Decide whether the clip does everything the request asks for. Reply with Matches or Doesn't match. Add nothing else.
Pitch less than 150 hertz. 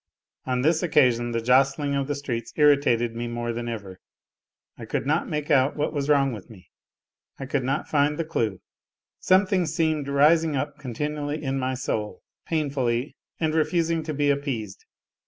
Matches